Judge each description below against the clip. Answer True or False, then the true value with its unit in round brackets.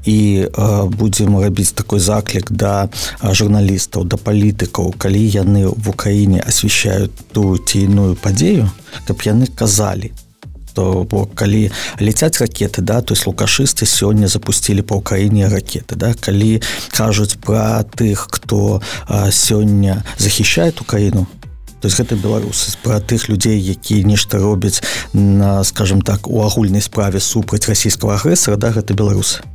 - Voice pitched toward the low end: True (105 Hz)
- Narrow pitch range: True (1.6 semitones)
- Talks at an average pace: True (125 wpm)